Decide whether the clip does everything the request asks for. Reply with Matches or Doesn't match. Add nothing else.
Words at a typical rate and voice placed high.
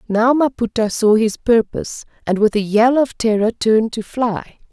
Matches